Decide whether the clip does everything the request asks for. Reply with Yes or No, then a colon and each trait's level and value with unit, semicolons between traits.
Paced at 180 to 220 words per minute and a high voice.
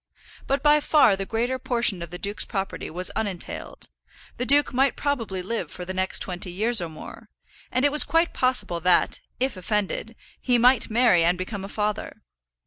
Yes: average, 185 wpm; high, 210 Hz